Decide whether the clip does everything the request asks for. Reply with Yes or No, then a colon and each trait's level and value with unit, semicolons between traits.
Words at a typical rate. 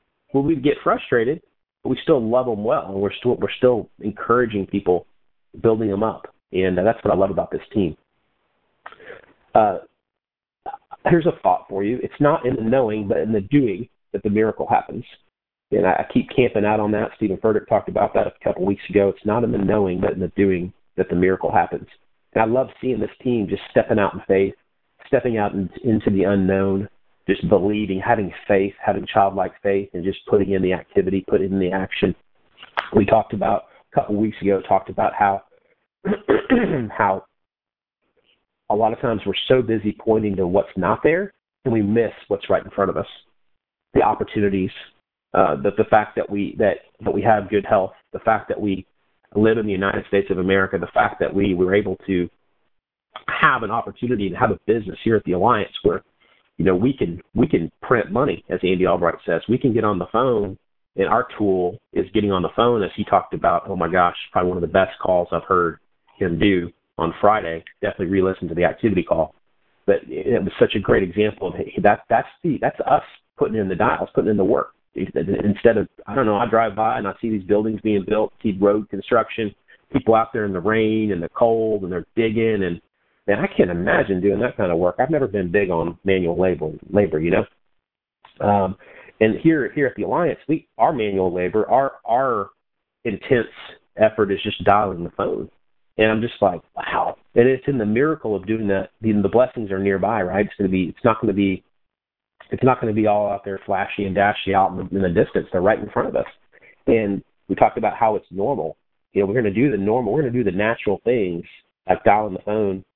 No: fast, 215 wpm